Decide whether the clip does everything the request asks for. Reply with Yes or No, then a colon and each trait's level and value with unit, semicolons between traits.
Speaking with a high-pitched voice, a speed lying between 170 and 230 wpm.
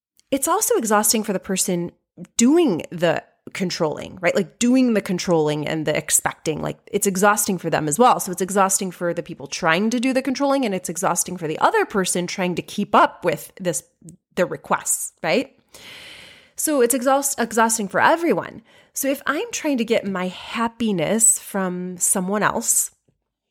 Yes: high, 195 Hz; average, 175 wpm